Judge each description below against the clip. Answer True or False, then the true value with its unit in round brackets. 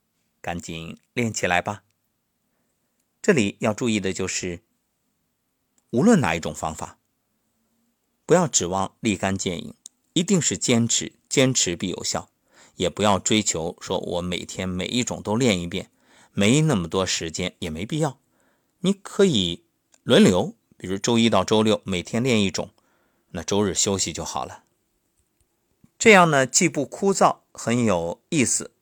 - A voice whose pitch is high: False (105 Hz)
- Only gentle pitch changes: False (5.6 semitones)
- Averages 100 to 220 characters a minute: True (210 characters per minute)